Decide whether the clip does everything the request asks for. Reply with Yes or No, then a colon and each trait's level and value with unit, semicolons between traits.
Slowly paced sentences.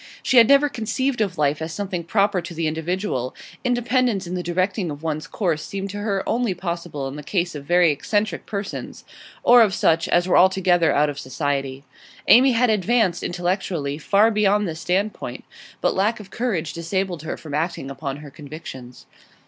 No: average, 180 wpm